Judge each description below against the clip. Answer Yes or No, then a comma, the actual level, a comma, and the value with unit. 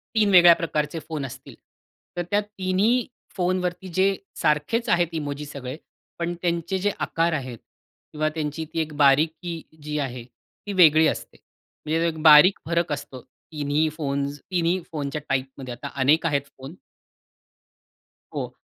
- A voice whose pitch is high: No, medium, 155 Hz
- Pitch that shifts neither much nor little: Yes, average, 3.6 semitones